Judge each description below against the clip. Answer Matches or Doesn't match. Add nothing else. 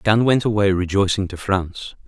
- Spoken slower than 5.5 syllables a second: Matches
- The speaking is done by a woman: Doesn't match